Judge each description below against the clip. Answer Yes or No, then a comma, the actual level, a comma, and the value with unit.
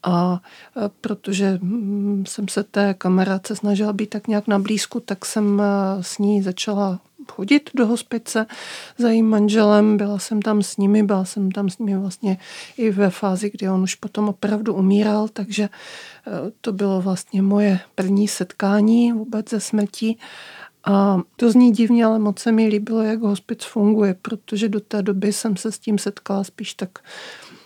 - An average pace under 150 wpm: No, average, 165 wpm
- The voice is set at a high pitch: Yes, high, 210 Hz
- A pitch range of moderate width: No, narrow, 1.9 semitones